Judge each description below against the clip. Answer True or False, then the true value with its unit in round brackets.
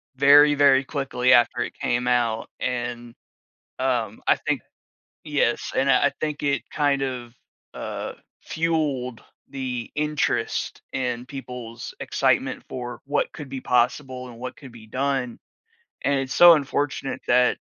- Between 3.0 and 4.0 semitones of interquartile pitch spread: False (2.6 semitones)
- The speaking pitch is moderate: False (130 Hz)